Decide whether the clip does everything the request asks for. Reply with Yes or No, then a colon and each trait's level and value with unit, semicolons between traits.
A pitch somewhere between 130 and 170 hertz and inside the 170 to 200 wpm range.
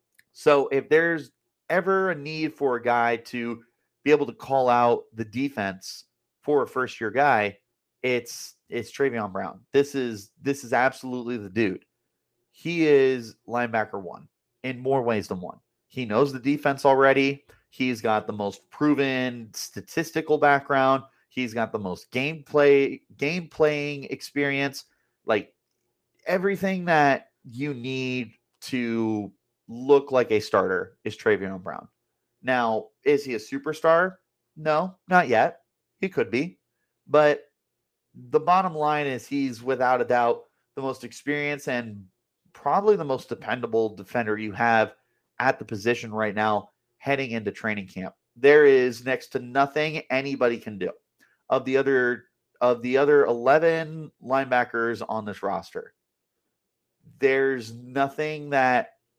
No: low, 135 Hz; average, 140 wpm